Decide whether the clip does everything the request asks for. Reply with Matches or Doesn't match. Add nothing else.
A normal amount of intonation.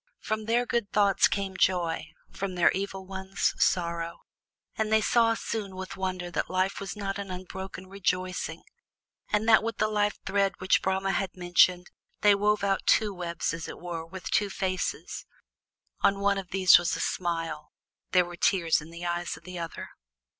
Doesn't match